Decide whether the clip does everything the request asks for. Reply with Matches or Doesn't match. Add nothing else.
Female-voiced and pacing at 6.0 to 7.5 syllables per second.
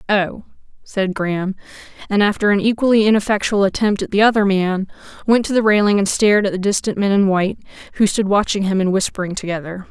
Matches